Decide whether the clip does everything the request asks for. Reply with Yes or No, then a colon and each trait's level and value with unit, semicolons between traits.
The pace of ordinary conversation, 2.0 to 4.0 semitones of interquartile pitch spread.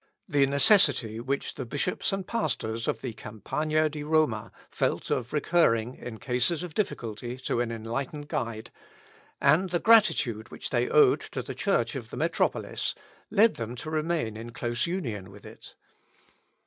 No: average, 160 wpm; wide, 5.6 semitones